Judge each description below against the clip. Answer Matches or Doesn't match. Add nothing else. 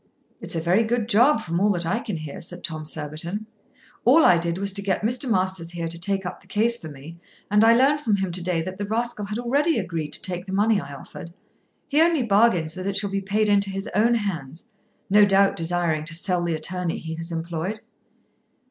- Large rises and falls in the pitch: Doesn't match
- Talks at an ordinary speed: Doesn't match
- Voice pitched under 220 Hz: Matches